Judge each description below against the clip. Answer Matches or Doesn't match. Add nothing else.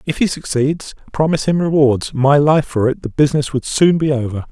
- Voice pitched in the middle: Matches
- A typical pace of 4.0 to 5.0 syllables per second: Doesn't match